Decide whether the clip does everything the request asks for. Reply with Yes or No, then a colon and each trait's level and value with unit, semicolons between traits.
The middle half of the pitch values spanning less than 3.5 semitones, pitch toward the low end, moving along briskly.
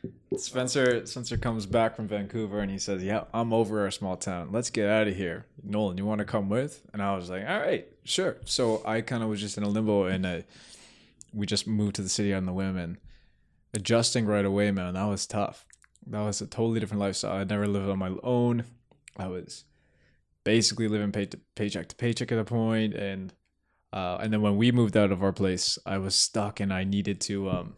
Yes: narrow, 2.5 semitones; low, 105 Hz; fast, 225 wpm